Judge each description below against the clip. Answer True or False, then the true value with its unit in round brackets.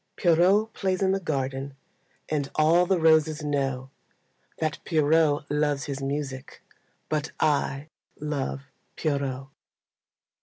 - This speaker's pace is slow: True (110 wpm)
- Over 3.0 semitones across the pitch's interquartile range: False (2.7 semitones)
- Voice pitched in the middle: True (150 Hz)